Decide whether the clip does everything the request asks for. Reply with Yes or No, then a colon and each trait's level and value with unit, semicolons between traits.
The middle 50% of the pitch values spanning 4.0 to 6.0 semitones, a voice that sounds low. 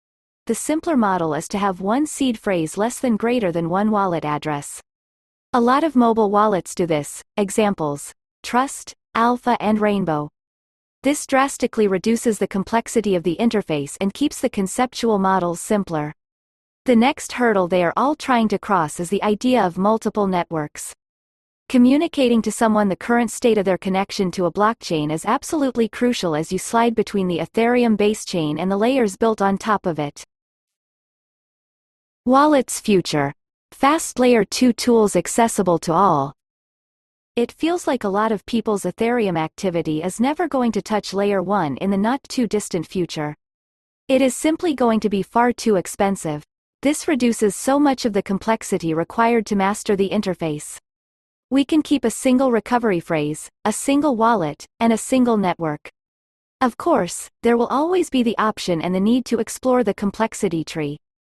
No: average, 5.2 semitones; high, 210 Hz